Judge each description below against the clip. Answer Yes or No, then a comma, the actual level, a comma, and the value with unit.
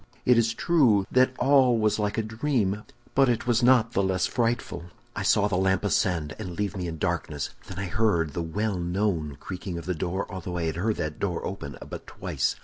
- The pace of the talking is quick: Yes, fast, 215 wpm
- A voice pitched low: Yes, low, 100 Hz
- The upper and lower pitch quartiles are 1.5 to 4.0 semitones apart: No, average, 4.4 semitones